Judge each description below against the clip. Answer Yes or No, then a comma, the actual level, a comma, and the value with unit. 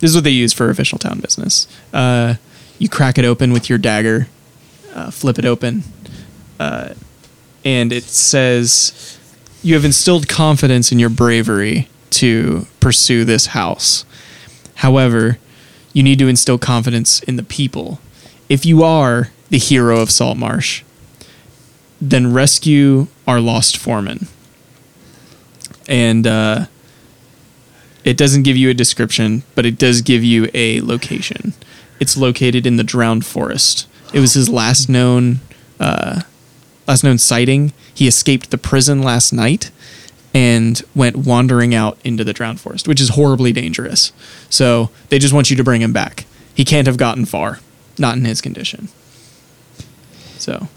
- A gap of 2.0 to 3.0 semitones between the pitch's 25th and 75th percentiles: Yes, narrow, 2.6 semitones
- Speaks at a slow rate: No, average, 150 wpm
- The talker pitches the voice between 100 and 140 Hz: Yes, low, 125 Hz